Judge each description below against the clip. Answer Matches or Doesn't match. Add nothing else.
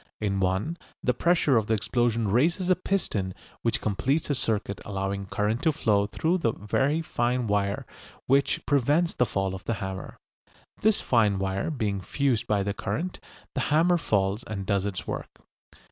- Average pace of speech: Matches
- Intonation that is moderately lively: Doesn't match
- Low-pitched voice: Matches